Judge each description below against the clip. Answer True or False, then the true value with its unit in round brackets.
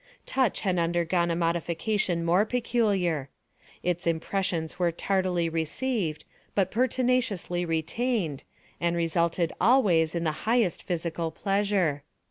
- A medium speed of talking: False (110 wpm)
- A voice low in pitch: False (175 Hz)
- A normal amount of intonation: True (3.6 semitones)